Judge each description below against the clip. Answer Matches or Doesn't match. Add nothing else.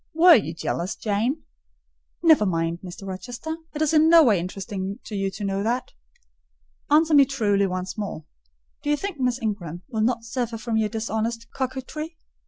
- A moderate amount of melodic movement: Doesn't match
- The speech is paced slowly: Doesn't match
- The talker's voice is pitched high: Matches